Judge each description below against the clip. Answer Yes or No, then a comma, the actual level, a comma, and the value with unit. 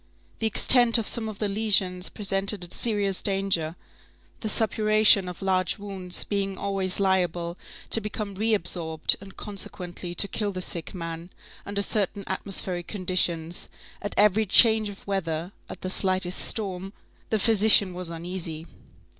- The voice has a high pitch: Yes, high, 195 Hz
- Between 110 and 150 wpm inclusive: Yes, average, 145 wpm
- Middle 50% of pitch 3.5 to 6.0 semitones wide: No, narrow, 2.6 semitones